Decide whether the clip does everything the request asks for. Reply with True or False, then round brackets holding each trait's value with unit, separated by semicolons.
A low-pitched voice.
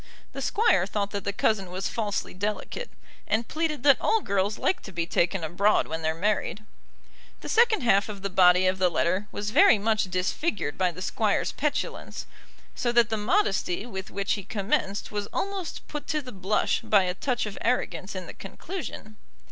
False (205 Hz)